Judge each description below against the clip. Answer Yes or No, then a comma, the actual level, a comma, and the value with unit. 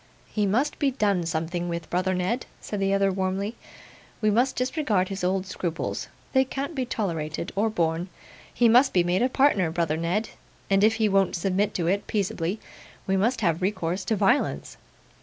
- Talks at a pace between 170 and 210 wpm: Yes, average, 180 wpm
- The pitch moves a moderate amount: Yes, average, 4.0 semitones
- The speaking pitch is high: Yes, high, 195 Hz